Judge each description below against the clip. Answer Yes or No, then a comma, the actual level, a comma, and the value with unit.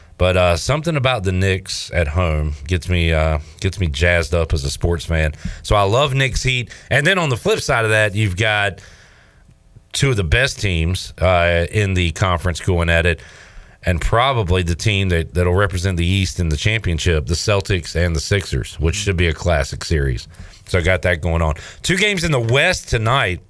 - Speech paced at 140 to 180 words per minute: No, fast, 205 wpm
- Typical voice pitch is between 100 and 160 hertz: No, very low, 90 Hz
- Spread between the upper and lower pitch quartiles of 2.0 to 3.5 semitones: No, average, 3.9 semitones